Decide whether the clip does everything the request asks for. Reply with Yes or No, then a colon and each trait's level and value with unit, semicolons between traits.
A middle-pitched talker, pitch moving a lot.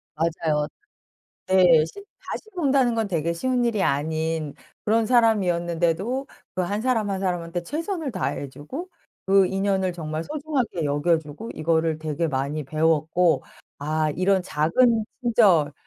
Yes: medium, 175 Hz; wide, 6.3 semitones